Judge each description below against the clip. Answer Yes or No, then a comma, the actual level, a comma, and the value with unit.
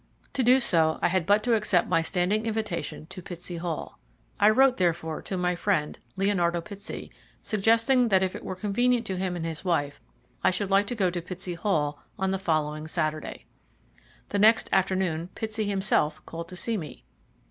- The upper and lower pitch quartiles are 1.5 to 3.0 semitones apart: No, average, 3.8 semitones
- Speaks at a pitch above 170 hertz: Yes, medium, 185 Hz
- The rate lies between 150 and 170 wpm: No, average, 185 wpm